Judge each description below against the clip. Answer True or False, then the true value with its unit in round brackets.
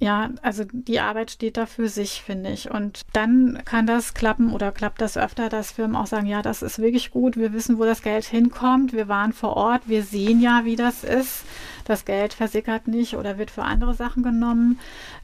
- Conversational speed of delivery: False (215 wpm)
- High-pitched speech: True (225 Hz)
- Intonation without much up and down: True (1.9 semitones)